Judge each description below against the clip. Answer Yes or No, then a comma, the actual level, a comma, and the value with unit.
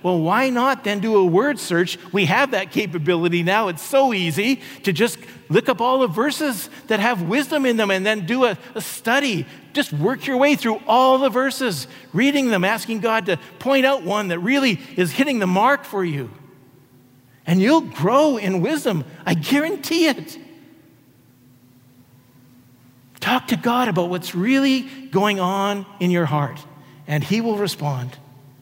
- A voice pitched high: Yes, high, 200 Hz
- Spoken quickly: No, average, 170 wpm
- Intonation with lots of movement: Yes, wide, 8.9 semitones